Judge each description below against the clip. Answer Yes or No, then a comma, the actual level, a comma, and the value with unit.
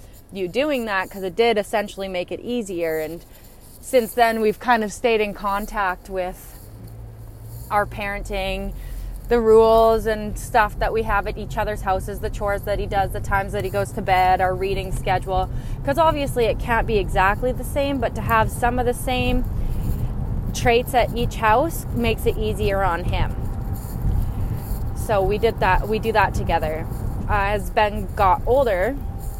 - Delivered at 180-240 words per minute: No, average, 170 wpm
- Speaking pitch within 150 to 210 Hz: Yes, medium, 185 Hz